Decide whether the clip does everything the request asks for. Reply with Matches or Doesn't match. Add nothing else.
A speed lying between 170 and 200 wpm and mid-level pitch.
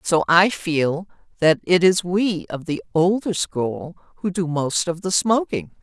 Matches